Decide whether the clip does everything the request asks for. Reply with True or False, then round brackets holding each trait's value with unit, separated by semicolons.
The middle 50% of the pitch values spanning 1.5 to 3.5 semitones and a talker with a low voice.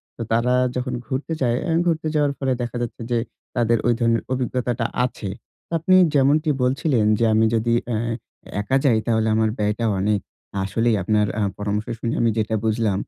True (2.7 semitones; 115 Hz)